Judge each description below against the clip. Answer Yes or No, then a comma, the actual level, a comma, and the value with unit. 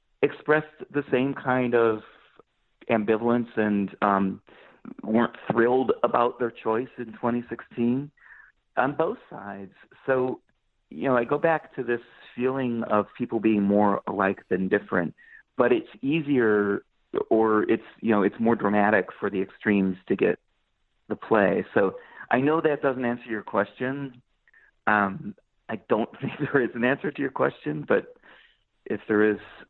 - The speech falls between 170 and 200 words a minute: No, average, 150 wpm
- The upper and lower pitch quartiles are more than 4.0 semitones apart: No, average, 3.7 semitones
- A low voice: Yes, low, 120 Hz